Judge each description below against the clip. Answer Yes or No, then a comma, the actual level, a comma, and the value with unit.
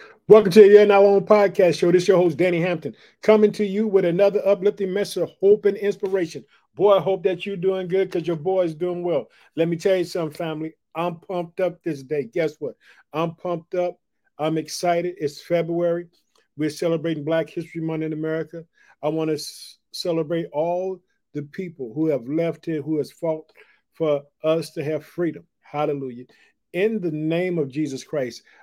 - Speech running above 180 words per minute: Yes, average, 190 wpm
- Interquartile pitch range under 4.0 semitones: Yes, average, 3.2 semitones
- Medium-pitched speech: Yes, medium, 170 Hz